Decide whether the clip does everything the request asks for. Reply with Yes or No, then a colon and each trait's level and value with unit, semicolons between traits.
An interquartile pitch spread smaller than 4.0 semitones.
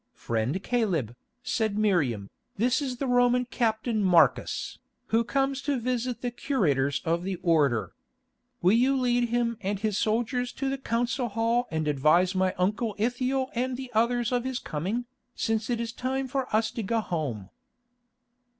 No: average, 5.0 semitones